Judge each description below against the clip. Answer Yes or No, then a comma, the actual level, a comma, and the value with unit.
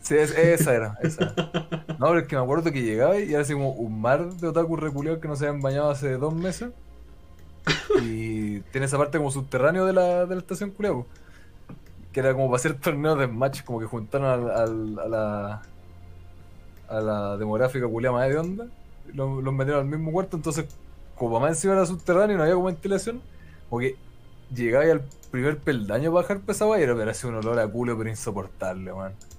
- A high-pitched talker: No, low, 135 Hz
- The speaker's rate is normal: No, fast, 205 wpm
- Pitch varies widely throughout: Yes, wide, 6.8 semitones